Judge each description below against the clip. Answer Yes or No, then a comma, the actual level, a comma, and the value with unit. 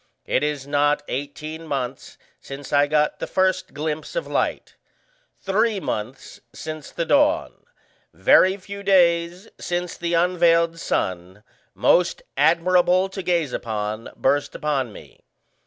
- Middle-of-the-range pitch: Yes, medium, 165 Hz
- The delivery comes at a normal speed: No, slow, 125 wpm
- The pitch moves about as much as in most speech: Yes, average, 4.2 semitones